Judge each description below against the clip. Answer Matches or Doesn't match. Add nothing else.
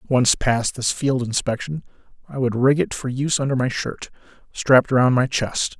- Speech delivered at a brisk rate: Doesn't match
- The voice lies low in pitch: Matches